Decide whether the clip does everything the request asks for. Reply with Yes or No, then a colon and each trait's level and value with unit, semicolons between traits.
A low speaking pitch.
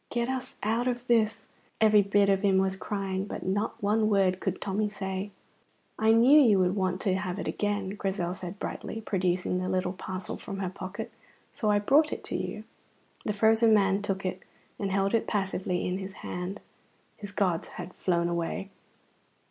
No: high, 195 Hz